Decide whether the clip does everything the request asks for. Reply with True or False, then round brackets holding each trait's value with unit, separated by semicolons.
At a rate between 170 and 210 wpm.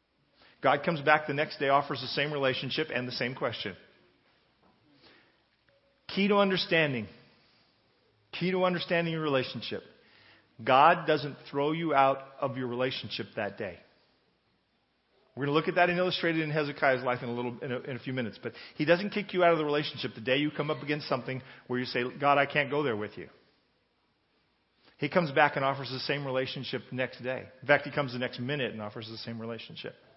True (205 wpm)